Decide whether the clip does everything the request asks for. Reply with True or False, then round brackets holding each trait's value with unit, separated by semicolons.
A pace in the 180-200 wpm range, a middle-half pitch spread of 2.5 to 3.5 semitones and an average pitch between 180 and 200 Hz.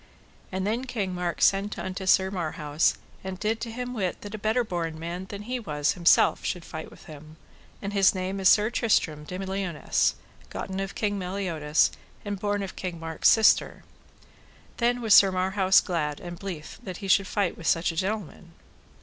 True (185 wpm; 3.2 semitones; 190 Hz)